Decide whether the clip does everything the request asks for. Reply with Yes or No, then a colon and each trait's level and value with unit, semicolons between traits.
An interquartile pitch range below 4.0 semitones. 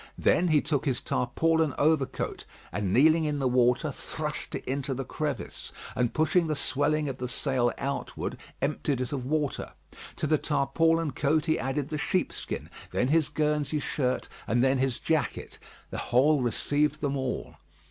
Yes: average, 3.0 semitones